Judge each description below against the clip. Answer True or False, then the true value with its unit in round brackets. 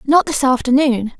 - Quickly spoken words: False (150 wpm)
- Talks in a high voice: True (265 Hz)